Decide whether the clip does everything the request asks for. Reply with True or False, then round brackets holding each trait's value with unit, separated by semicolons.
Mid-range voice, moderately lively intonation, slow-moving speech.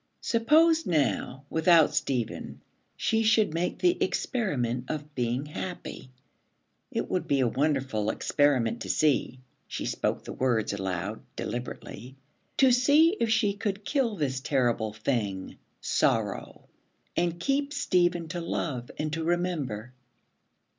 False (150 Hz; 8.2 semitones; 125 wpm)